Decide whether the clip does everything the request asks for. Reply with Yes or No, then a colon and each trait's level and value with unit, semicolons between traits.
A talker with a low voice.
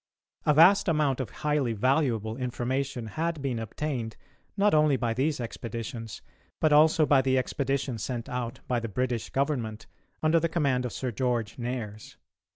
Yes: low, 130 Hz